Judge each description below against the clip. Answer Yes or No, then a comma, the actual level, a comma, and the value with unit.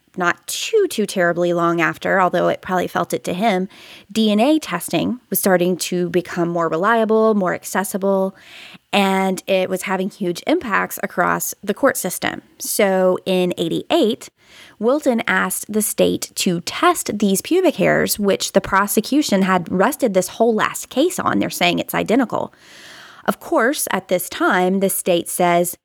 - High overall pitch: Yes, high, 195 Hz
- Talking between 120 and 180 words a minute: Yes, average, 155 wpm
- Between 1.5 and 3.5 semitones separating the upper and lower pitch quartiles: No, average, 4.0 semitones